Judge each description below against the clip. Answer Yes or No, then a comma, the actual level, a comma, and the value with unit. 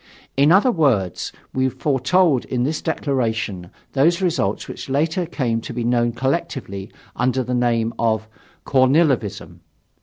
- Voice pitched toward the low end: Yes, low, 130 Hz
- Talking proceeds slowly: Yes, slow, 130 wpm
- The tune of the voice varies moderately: Yes, average, 4.7 semitones